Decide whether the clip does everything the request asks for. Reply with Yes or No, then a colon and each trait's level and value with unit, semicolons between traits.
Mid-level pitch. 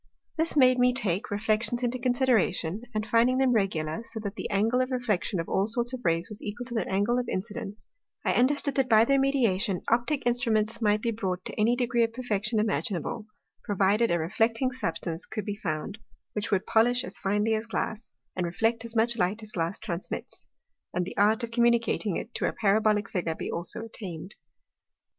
No: high, 220 Hz